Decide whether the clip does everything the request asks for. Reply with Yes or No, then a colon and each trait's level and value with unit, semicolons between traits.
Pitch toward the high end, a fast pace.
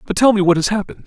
Yes: high, 200 Hz; fast, 335 wpm